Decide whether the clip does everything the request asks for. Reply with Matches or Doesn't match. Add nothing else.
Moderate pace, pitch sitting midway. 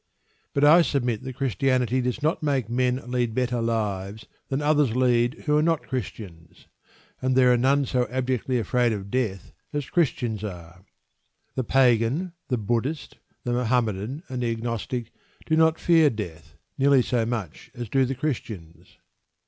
Doesn't match